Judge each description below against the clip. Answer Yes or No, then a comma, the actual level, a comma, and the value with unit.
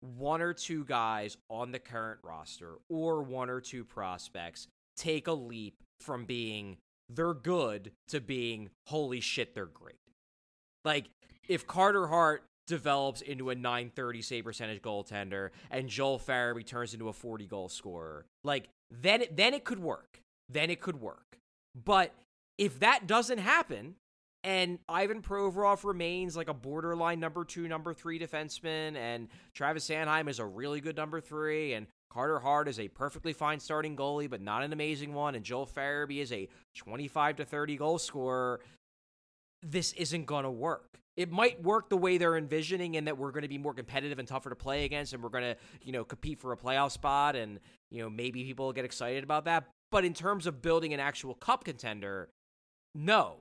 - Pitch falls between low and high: Yes, medium, 145 Hz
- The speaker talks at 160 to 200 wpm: Yes, average, 185 wpm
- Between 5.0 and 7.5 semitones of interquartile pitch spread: Yes, average, 5.3 semitones